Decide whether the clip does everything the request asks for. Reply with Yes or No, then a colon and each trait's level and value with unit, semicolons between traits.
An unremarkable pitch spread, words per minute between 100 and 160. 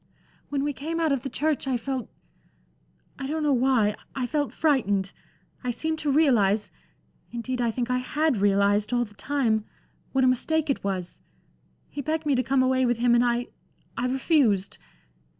No: average, 3.7 semitones; average, 180 wpm